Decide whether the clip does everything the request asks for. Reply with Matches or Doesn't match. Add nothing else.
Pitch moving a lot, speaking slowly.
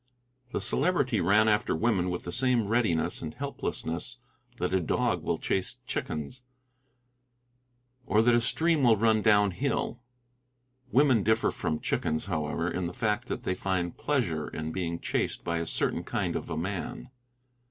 Doesn't match